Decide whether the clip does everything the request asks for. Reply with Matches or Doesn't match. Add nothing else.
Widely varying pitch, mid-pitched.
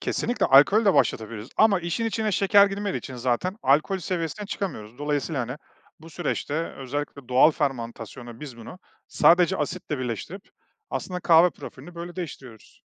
Matches